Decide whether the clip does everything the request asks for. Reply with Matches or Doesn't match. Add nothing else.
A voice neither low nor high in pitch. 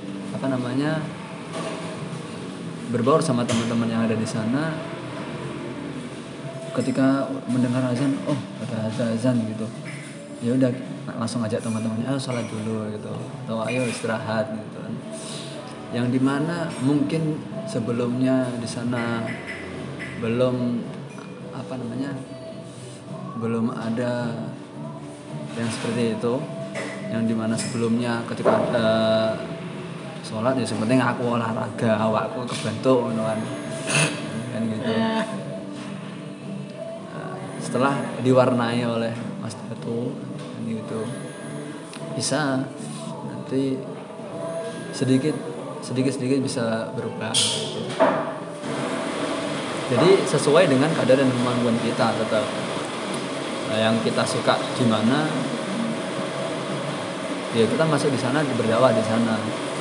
Doesn't match